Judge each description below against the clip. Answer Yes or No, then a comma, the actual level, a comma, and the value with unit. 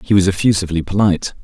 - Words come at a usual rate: Yes, average, 170 wpm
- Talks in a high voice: No, very low, 95 Hz